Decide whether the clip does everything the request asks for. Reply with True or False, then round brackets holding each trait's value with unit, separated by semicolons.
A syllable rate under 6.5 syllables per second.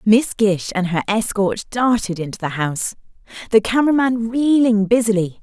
True (5.0 syllables/s)